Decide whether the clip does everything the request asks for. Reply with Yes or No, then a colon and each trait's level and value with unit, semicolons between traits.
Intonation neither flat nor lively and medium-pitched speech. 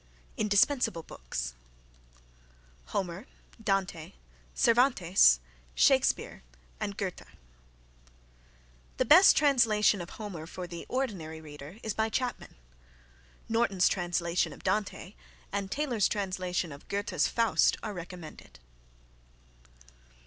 No: average, 4.4 semitones; high, 195 Hz